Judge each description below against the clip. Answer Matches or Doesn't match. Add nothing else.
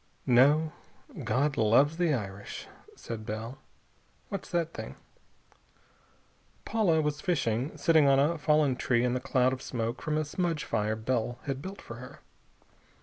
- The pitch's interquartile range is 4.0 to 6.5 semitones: Matches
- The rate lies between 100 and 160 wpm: Matches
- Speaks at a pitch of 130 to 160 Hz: Matches